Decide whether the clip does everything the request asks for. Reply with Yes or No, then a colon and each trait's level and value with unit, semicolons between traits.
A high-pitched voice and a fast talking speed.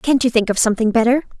Yes: high, 240 Hz; fast, 255 wpm